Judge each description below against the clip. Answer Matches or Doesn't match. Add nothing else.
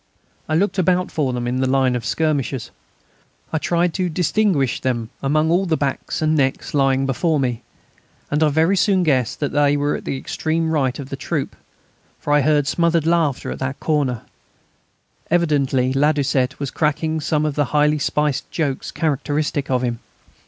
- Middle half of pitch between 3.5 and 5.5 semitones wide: Doesn't match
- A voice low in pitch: Doesn't match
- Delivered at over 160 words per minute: Matches